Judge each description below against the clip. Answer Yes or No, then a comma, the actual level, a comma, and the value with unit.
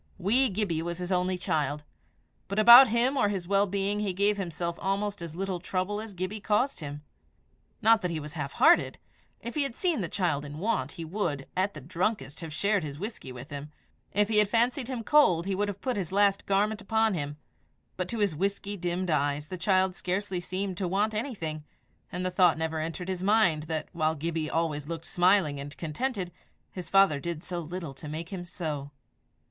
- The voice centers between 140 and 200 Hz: Yes, medium, 185 Hz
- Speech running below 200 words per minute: No, fast, 205 wpm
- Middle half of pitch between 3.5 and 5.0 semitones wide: Yes, average, 4.1 semitones